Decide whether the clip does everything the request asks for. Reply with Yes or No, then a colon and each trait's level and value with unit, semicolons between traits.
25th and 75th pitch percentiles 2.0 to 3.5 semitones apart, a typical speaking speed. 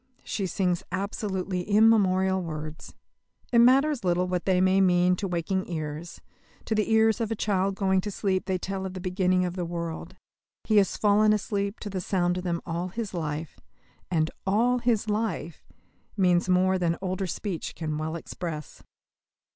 Yes: average, 2.7 semitones; average, 170 wpm